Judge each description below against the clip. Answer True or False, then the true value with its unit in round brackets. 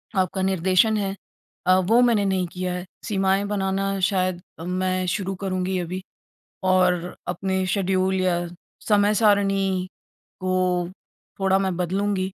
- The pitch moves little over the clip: True (1.1 semitones)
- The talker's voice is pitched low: False (190 Hz)